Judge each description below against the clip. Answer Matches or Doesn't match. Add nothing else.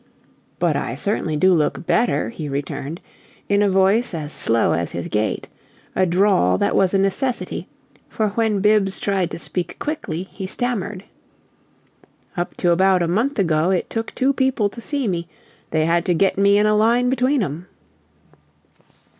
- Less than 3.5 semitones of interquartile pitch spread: Doesn't match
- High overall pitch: Matches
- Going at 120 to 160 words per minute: Doesn't match